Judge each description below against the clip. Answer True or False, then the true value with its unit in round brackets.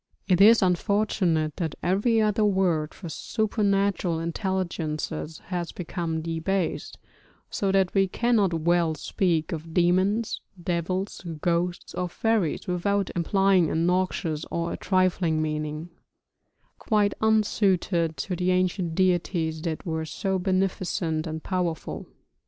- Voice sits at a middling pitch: True (180 Hz)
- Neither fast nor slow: False (120 wpm)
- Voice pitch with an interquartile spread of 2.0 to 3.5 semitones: True (2.9 semitones)